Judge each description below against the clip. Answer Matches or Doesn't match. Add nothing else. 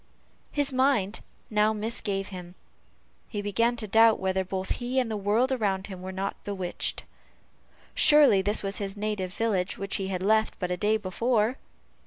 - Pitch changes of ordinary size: Matches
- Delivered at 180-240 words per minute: Doesn't match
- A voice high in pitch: Matches